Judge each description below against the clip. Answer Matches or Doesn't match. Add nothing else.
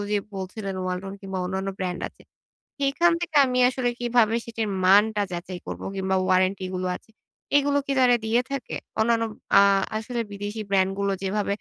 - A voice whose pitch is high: Matches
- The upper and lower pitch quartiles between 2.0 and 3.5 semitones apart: Doesn't match